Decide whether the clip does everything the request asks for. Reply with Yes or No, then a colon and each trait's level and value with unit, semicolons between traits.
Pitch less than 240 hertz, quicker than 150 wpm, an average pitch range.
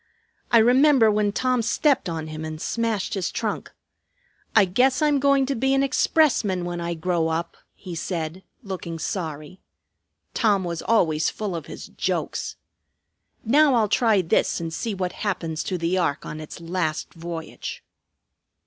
No: medium, 185 Hz; average, 160 wpm; wide, 5.8 semitones